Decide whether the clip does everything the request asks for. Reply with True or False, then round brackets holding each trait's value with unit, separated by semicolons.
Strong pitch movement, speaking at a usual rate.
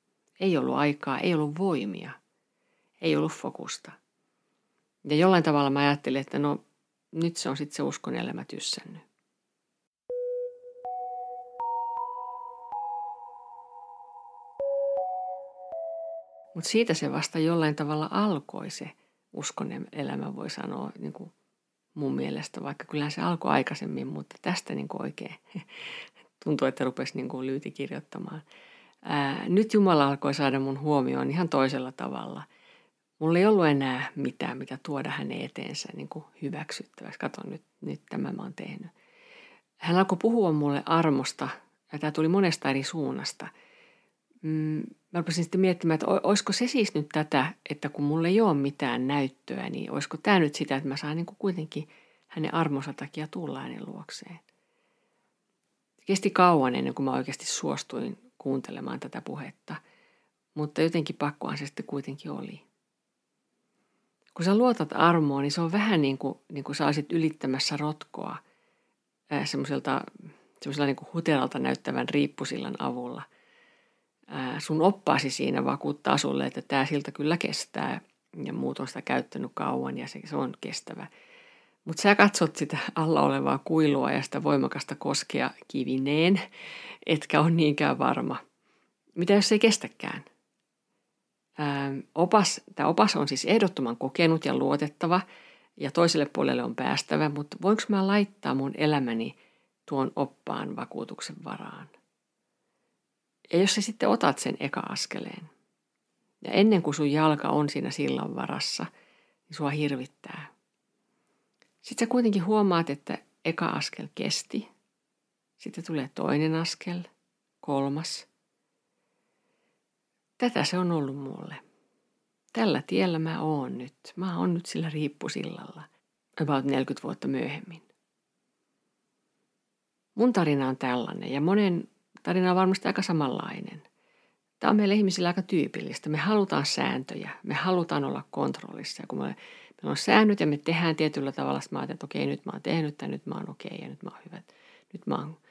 True (6.2 semitones; 140 wpm)